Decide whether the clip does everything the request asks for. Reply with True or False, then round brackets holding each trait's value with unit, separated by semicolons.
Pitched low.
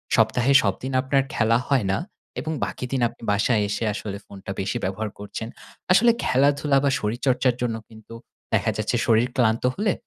True (120 Hz)